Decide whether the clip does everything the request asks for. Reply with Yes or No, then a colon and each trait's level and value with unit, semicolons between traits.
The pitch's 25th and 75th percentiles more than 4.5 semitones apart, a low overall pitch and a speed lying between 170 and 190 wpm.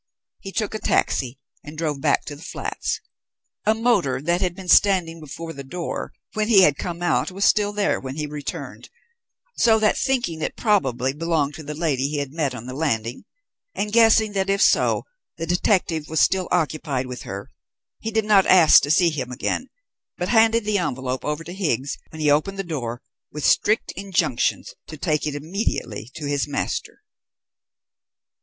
No: wide, 5.6 semitones; medium, 165 Hz; average, 185 wpm